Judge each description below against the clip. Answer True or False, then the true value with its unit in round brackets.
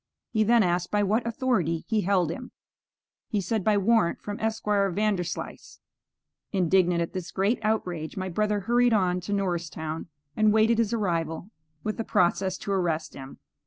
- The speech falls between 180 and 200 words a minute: False (165 wpm)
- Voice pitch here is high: True (200 Hz)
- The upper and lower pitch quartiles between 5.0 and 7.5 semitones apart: False (3.6 semitones)